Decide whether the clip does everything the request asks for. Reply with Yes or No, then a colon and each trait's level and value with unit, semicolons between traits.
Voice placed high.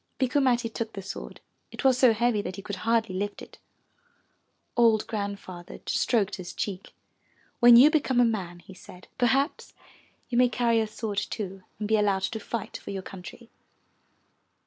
Yes: high, 220 Hz